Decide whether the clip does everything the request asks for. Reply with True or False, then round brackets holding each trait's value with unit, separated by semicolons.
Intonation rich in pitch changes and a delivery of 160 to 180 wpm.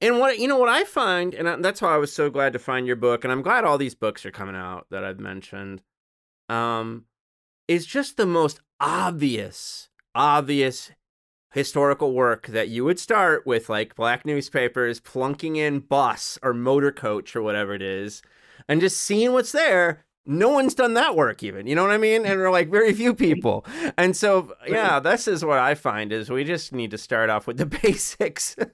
False (8.3 semitones; 205 wpm)